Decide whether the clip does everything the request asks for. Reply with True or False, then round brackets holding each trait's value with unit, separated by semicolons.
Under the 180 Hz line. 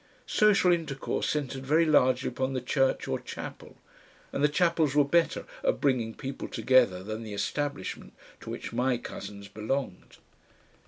True (135 Hz)